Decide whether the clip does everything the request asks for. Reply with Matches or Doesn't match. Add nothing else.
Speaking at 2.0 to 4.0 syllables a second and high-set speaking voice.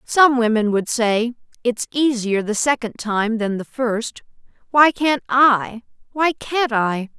Matches